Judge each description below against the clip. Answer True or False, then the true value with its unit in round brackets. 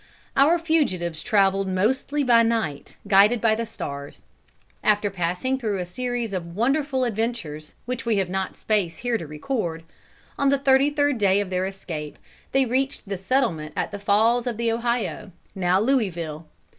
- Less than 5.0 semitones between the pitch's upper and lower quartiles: False (5.4 semitones)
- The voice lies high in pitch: True (215 Hz)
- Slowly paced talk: False (165 wpm)